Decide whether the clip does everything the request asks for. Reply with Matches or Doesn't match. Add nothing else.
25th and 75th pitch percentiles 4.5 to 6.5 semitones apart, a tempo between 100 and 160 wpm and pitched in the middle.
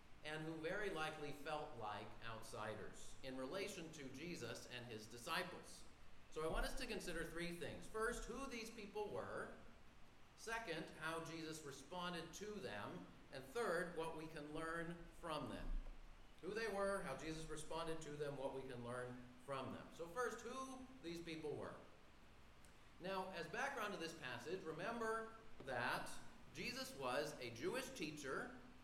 Matches